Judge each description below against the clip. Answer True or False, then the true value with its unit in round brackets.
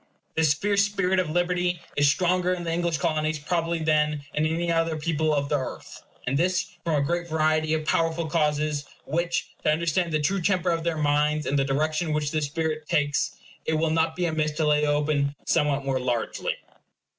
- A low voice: False (155 Hz)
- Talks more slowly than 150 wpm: False (195 wpm)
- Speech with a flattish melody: True (2.2 semitones)